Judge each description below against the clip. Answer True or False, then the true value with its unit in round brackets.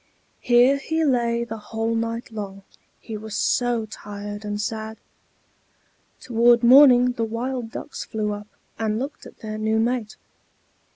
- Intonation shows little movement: True (2.1 semitones)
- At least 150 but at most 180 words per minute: False (140 wpm)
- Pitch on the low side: False (225 Hz)